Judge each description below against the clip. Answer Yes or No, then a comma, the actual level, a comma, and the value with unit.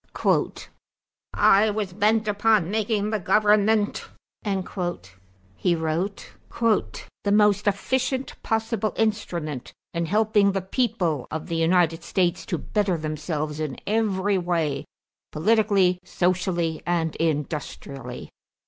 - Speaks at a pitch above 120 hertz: Yes, high, 190 Hz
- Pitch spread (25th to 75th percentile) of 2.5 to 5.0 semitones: Yes, average, 4.3 semitones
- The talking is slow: Yes, slow, 105 wpm